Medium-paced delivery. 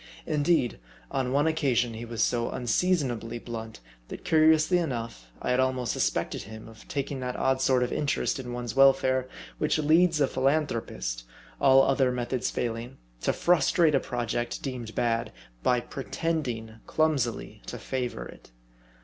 Yes: average, 150 wpm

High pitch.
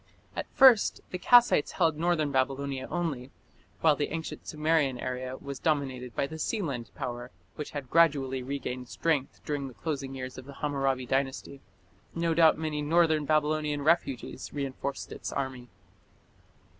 No: medium, 140 Hz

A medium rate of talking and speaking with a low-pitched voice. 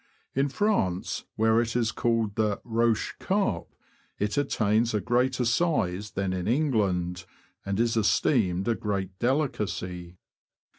No: slow, 130 wpm; low, 110 Hz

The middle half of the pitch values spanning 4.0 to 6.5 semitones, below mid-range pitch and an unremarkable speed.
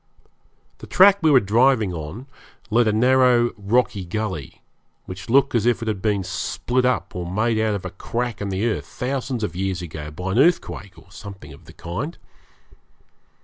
Yes: average, 4.8 semitones; low, 110 Hz; average, 190 wpm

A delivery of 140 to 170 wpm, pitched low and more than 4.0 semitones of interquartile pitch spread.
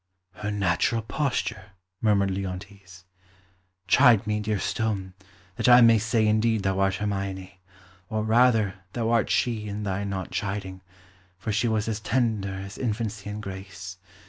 No: average, 145 wpm; low, 105 Hz; narrow, 2.4 semitones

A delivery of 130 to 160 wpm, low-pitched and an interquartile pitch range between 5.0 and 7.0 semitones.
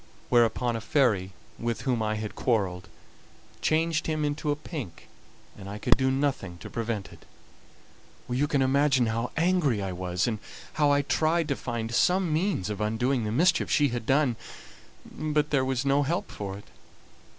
No: average, 175 wpm; low, 130 Hz; average, 5.3 semitones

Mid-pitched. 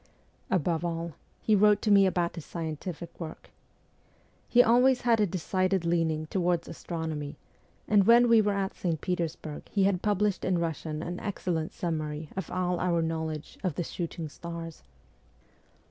Yes: medium, 175 Hz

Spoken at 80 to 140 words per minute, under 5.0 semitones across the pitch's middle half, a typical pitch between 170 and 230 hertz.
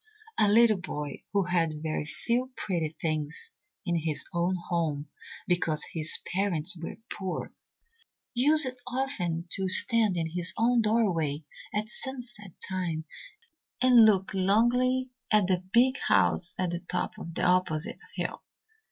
No: slow, 135 wpm; wide, 5.4 semitones; medium, 185 Hz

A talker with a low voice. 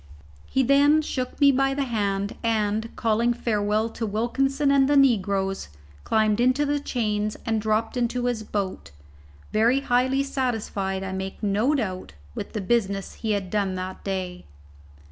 No: high, 220 Hz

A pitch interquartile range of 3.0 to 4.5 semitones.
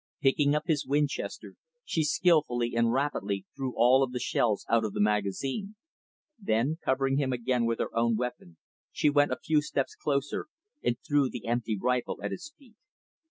Yes: average, 4.0 semitones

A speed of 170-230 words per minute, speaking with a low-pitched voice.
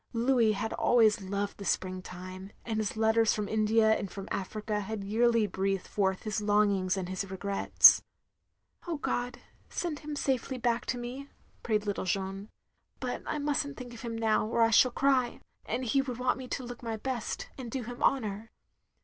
No: average, 195 wpm; high, 220 Hz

